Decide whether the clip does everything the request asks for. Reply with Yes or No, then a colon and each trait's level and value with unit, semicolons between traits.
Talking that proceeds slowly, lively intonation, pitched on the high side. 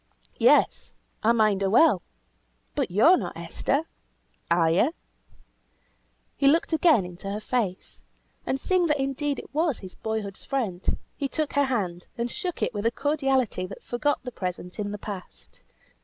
No: average, 165 wpm; wide, 6.6 semitones; high, 235 Hz